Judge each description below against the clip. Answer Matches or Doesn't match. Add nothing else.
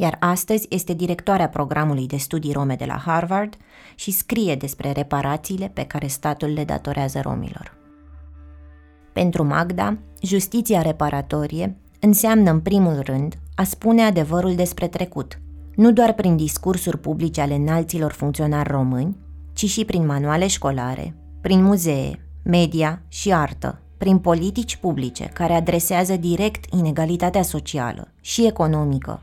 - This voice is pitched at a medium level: Matches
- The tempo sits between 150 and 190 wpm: Doesn't match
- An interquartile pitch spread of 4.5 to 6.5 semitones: Matches